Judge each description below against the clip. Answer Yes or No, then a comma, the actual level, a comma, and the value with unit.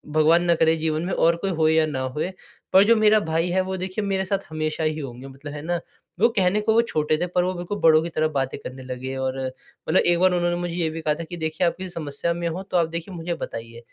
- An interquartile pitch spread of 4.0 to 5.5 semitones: No, average, 2.8 semitones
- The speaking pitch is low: No, medium, 165 Hz